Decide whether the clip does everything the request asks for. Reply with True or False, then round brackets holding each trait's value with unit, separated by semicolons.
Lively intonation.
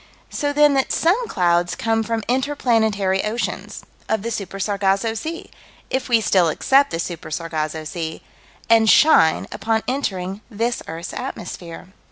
True (5.7 semitones)